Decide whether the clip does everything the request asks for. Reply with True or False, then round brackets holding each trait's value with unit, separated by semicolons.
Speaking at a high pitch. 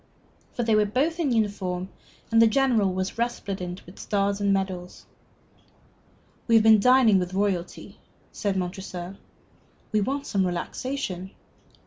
True (200 Hz)